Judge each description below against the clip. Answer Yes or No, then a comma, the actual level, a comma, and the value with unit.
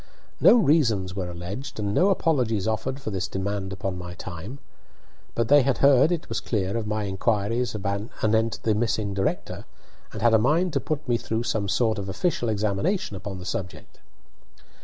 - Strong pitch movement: No, average, 4.2 semitones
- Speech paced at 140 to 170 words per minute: No, average, 180 wpm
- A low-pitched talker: Yes, low, 110 Hz